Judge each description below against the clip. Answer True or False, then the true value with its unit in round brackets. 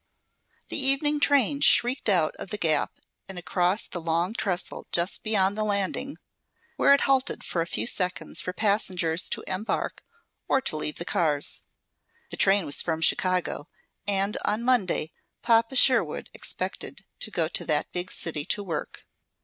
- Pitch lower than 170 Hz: False (195 Hz)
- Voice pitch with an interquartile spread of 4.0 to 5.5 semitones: True (5.1 semitones)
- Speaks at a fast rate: False (160 wpm)